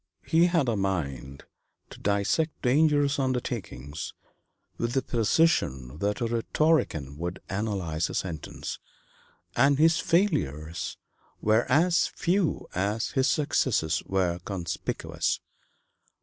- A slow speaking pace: Yes, slow, 105 wpm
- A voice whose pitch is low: Yes, low, 110 Hz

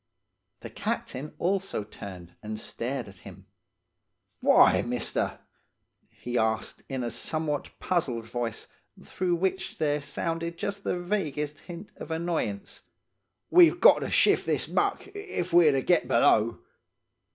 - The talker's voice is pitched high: No, medium, 150 Hz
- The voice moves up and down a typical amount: No, wide, 6.9 semitones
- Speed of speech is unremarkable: No, slow, 130 wpm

